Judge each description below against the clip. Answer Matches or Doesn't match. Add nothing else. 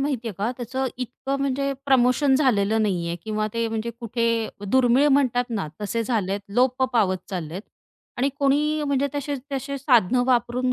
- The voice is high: Matches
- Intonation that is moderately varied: Matches